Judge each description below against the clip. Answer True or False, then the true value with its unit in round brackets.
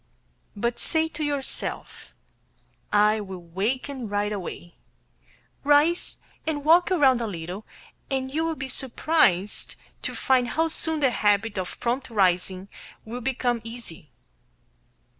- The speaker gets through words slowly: True (125 wpm)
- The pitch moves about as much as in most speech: False (5.9 semitones)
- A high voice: True (240 Hz)